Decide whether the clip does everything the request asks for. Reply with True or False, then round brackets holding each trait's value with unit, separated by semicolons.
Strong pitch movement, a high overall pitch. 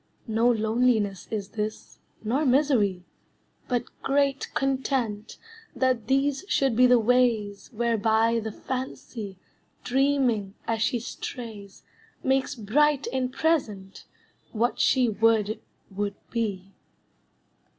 False (3.6 semitones; 230 Hz)